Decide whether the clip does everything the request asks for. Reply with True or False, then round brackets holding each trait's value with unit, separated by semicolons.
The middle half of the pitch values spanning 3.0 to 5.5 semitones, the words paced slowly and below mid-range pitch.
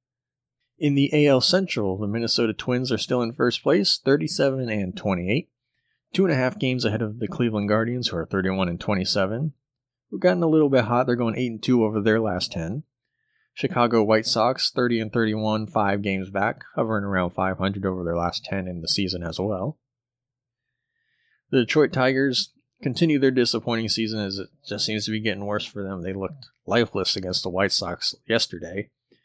False (4.1 semitones; 185 wpm; 115 Hz)